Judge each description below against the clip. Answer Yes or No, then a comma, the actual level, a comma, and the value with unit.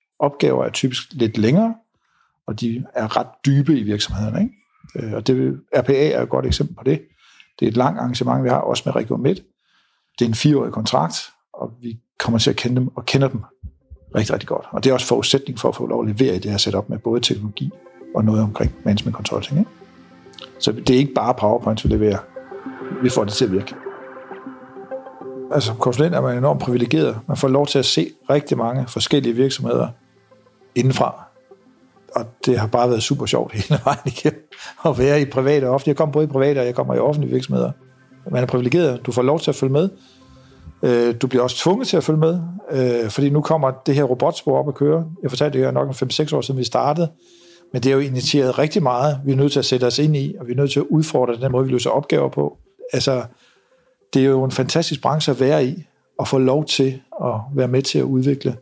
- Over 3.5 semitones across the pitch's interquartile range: No, average, 3.2 semitones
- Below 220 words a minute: No, fast, 225 wpm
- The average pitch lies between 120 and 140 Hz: Yes, low, 130 Hz